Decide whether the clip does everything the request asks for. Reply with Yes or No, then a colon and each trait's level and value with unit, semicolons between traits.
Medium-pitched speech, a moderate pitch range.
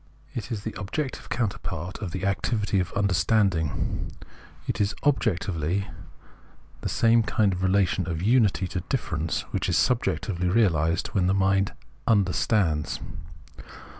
No: very low, 95 Hz; average, 3.4 semitones